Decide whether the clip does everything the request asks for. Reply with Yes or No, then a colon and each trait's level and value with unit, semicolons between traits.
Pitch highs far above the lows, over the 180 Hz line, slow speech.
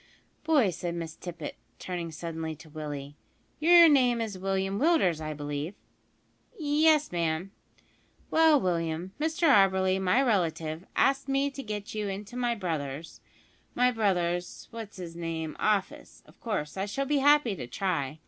No: wide, 7.3 semitones; high, 190 Hz; average, 150 wpm